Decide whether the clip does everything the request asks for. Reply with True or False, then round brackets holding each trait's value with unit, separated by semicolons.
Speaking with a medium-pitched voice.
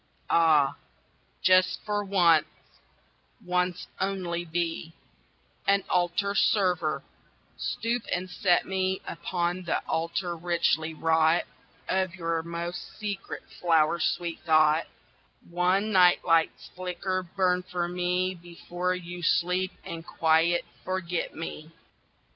True (175 Hz)